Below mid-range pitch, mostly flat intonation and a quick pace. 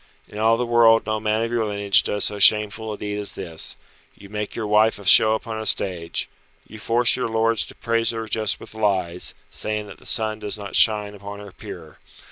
Yes: low, 105 Hz; narrow, 1.6 semitones; fast, 220 wpm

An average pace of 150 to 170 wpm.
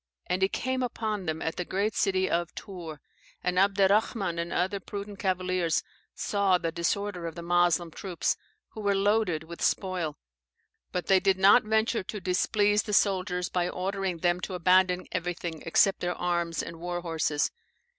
Yes: average, 165 wpm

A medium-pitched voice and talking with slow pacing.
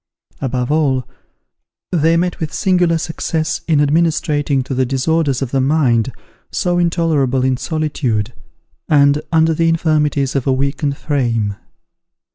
Yes: medium, 145 Hz; slow, 130 wpm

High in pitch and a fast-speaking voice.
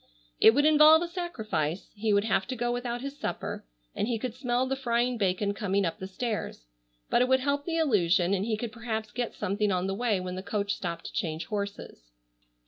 Yes: high, 220 Hz; fast, 220 wpm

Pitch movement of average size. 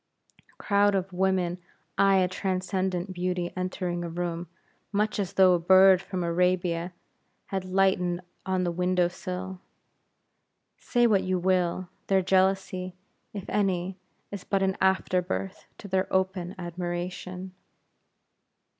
No: narrow, 1.1 semitones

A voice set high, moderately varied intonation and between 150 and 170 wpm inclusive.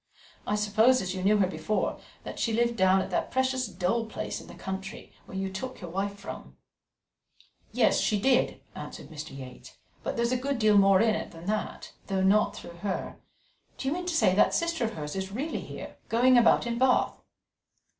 No: high, 210 Hz; average, 4.1 semitones; average, 200 wpm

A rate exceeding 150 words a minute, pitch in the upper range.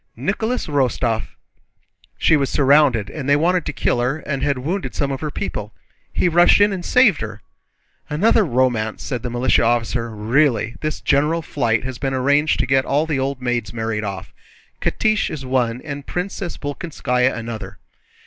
No: average, 170 wpm; low, 135 Hz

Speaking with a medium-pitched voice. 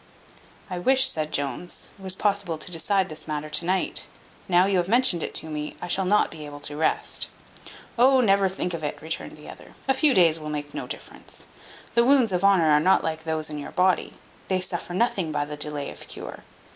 Yes: medium, 175 Hz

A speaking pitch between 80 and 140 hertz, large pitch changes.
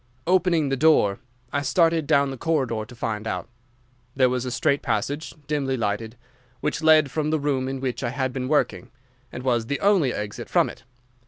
No: low, 135 Hz; average, 3.8 semitones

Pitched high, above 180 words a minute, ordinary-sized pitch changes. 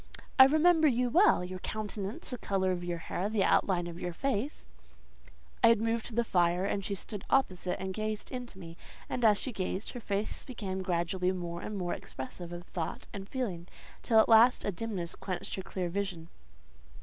Yes: high, 195 Hz; average, 190 wpm; average, 4.1 semitones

